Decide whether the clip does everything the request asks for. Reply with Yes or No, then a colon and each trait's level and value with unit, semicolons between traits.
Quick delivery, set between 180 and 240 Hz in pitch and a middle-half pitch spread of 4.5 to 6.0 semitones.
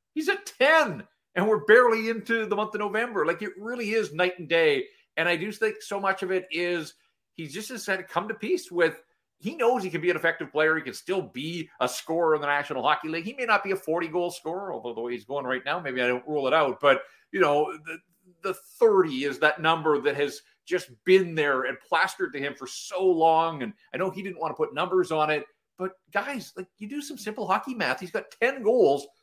Yes: fast, 245 wpm; medium, 185 Hz; average, 5.2 semitones